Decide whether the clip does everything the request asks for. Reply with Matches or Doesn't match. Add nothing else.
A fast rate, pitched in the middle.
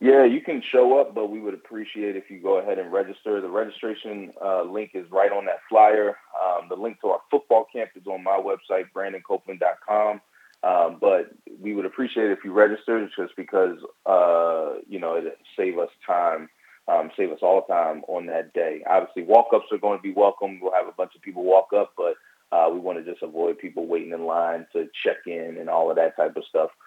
Doesn't match